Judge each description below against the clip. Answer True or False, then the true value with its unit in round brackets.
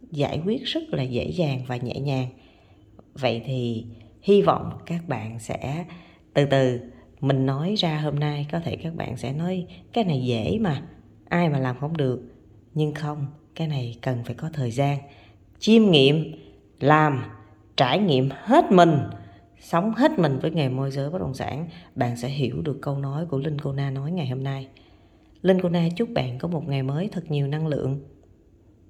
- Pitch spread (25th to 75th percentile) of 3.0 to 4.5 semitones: False (4.9 semitones)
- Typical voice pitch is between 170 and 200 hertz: False (140 Hz)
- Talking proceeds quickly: False (190 wpm)